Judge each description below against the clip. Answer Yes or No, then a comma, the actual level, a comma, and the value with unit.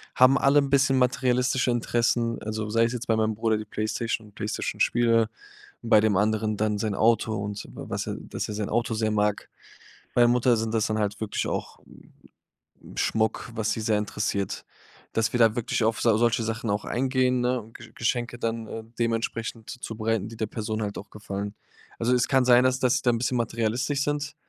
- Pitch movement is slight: Yes, narrow, 2.2 semitones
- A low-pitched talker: Yes, low, 115 Hz